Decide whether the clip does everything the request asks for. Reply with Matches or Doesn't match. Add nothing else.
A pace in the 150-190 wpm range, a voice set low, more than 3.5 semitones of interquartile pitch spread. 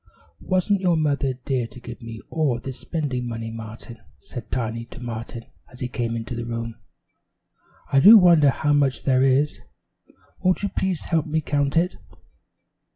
Matches